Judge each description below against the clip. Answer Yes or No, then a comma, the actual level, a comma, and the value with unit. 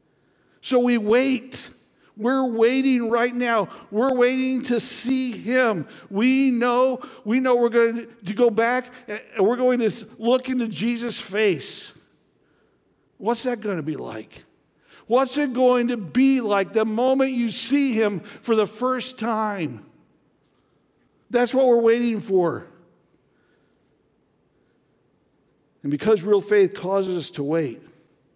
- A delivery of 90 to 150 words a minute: Yes, slow, 135 wpm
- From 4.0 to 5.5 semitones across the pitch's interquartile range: No, average, 3.0 semitones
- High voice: Yes, high, 235 Hz